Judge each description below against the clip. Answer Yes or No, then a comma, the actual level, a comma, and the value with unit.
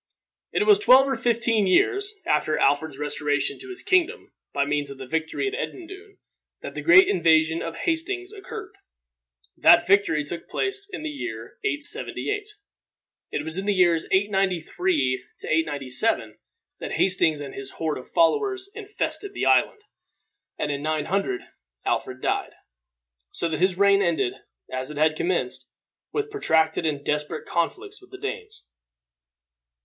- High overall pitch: Yes, high, 195 Hz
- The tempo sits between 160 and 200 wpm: No, average, 145 wpm